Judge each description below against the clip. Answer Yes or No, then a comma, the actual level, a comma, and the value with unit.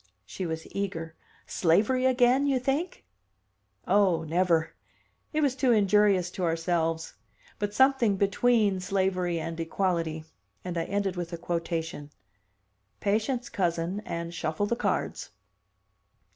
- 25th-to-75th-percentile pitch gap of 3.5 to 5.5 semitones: Yes, average, 4.2 semitones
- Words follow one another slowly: Yes, slow, 120 wpm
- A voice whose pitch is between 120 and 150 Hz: No, medium, 185 Hz